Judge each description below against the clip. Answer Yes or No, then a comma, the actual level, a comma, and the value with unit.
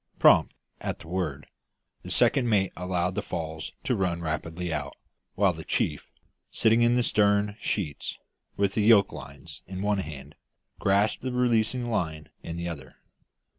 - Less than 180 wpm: Yes, average, 160 wpm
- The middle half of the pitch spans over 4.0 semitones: Yes, average, 4.8 semitones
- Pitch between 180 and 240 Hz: No, very low, 95 Hz